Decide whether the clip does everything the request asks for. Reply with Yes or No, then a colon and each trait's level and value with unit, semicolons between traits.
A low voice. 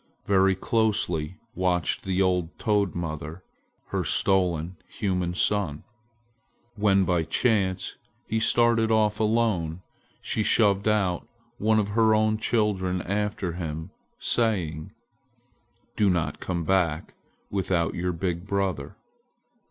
Yes: very low, 95 Hz